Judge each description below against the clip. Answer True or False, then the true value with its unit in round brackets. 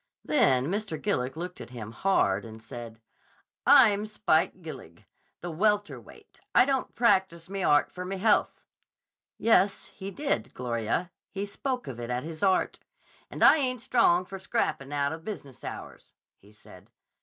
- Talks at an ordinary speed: True (155 wpm)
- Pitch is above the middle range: False (175 Hz)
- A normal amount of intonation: False (8.2 semitones)